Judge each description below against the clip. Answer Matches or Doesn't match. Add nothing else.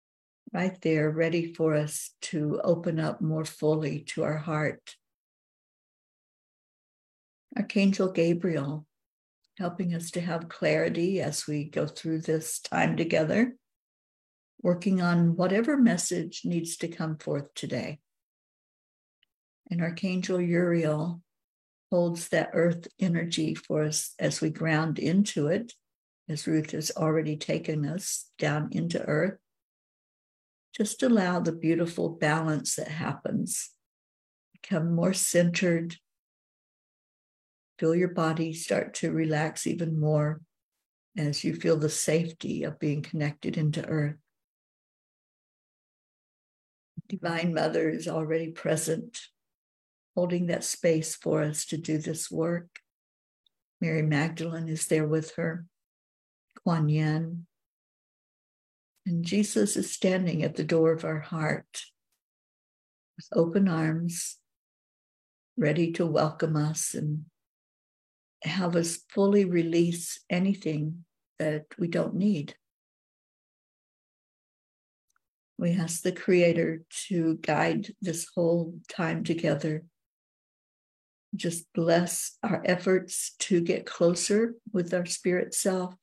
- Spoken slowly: Matches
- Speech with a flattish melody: Matches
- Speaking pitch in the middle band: Matches